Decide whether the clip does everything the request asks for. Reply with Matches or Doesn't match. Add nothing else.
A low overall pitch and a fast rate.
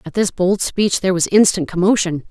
Doesn't match